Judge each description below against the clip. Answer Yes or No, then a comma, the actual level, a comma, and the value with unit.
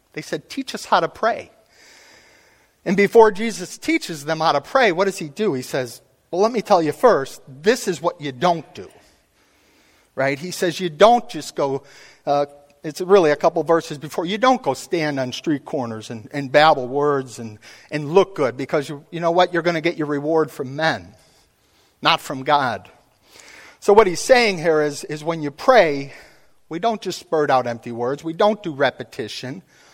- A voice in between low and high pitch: Yes, medium, 160 Hz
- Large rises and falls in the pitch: No, average, 4.4 semitones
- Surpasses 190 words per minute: Yes, average, 200 wpm